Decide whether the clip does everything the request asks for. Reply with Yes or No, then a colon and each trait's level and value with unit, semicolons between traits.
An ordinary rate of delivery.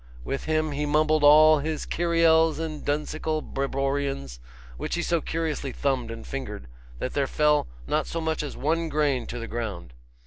Yes: average, 170 wpm